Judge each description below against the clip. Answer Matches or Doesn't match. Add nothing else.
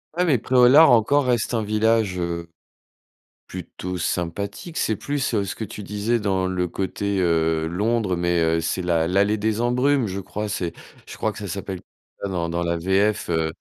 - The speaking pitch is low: Matches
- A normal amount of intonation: Matches